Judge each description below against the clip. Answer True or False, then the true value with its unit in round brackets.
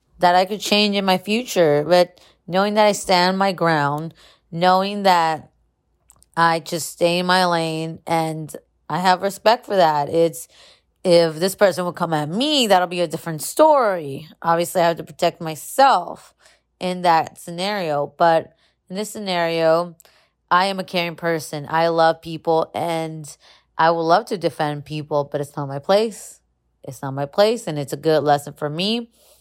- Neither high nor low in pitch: True (170 Hz)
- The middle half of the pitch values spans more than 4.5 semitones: False (3.0 semitones)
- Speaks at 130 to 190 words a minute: True (175 wpm)